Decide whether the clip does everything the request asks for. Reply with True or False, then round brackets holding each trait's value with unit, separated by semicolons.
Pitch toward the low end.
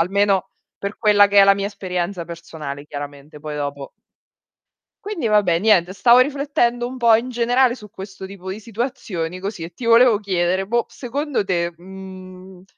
False (195 Hz)